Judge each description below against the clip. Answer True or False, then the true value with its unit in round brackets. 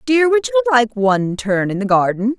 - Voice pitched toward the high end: True (230 Hz)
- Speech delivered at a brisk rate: True (225 wpm)